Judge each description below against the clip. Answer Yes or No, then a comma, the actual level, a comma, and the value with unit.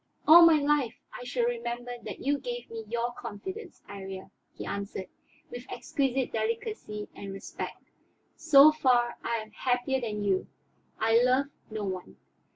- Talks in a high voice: Yes, high, 240 Hz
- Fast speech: No, average, 150 wpm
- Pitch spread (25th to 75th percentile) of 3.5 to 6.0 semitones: Yes, average, 3.8 semitones